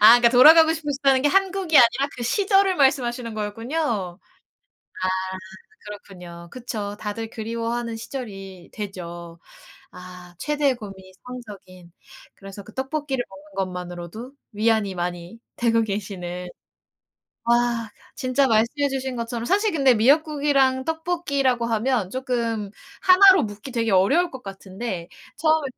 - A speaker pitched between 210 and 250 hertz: Yes, high, 235 Hz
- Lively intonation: Yes, wide, 5.7 semitones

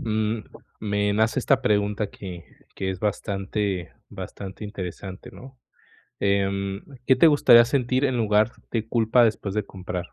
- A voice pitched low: Yes, low, 105 Hz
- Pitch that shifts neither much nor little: Yes, average, 3.0 semitones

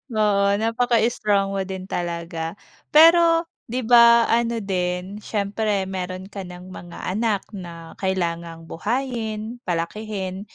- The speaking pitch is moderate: No, high, 200 Hz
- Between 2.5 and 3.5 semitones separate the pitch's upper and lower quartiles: No, average, 4.0 semitones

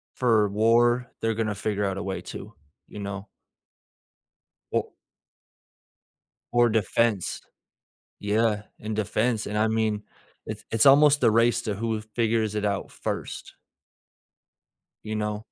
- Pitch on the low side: Yes, low, 110 Hz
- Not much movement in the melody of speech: Yes, narrow, 1.7 semitones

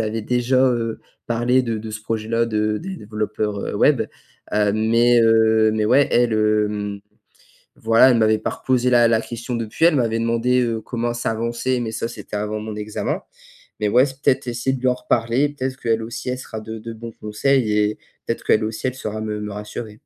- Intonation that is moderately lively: No, narrow, 2.2 semitones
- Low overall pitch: Yes, low, 115 Hz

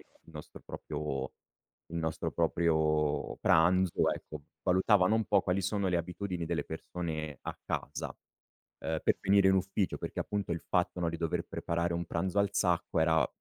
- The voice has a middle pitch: No, very low, 85 Hz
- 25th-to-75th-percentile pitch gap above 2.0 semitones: Yes, average, 2.7 semitones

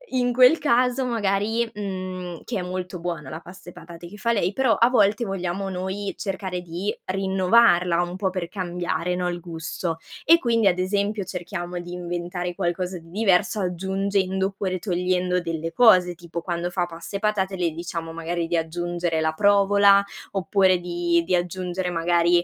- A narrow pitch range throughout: Yes, narrow, 2.3 semitones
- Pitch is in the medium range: Yes, medium, 180 Hz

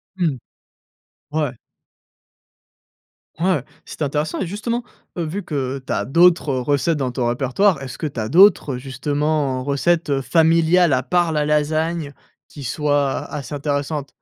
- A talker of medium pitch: Yes, medium, 150 Hz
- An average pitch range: Yes, average, 3.6 semitones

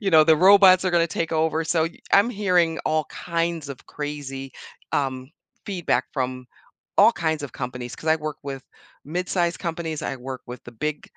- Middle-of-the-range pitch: Yes, medium, 160 Hz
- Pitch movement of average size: Yes, average, 4.0 semitones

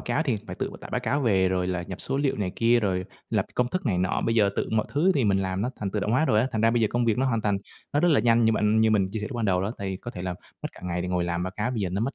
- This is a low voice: Yes, low, 110 Hz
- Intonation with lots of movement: No, average, 4.2 semitones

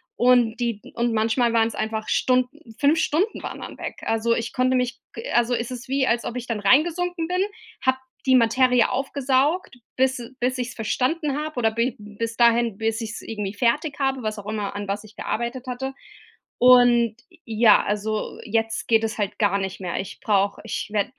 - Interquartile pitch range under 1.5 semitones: No, average, 2.9 semitones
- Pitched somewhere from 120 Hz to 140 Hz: No, high, 235 Hz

